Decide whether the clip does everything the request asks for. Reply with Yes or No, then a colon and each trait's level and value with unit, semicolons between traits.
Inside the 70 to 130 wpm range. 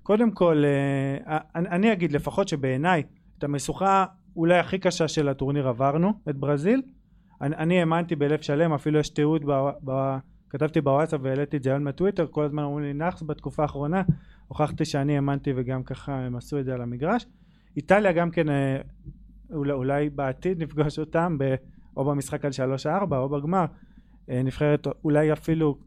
No: fast, 150 wpm